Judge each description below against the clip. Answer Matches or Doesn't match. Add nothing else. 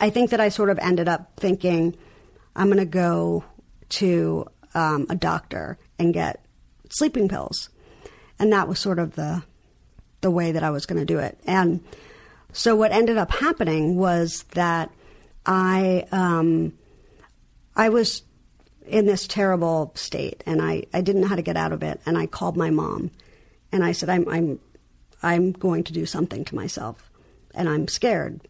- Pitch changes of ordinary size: Matches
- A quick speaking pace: Doesn't match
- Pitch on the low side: Doesn't match